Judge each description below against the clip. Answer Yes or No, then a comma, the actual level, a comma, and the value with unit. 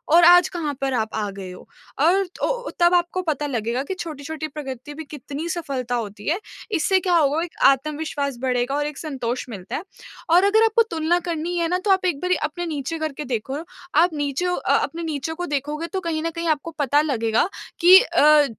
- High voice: Yes, very high, 310 Hz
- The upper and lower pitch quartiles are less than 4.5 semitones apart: Yes, average, 4.0 semitones